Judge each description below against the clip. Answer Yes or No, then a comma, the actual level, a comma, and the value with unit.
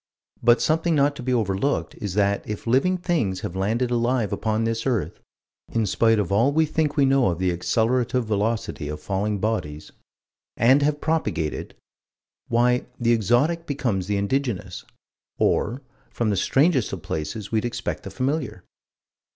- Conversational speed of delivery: Yes, average, 160 wpm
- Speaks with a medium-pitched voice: No, low, 115 Hz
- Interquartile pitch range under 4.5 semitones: No, average, 5.0 semitones